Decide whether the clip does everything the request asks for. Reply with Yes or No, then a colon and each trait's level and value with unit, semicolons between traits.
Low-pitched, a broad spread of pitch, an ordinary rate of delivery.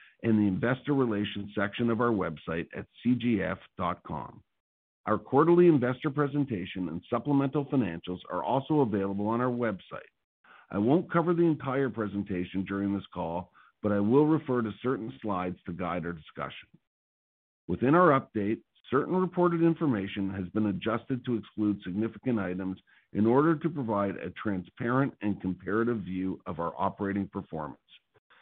Yes: low, 110 Hz; wide, 5.7 semitones; average, 145 wpm